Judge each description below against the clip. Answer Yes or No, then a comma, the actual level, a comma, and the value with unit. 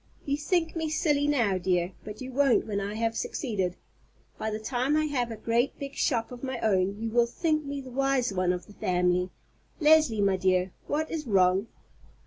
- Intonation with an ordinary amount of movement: No, wide, 6.3 semitones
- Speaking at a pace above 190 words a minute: Yes, average, 200 wpm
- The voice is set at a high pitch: Yes, high, 235 Hz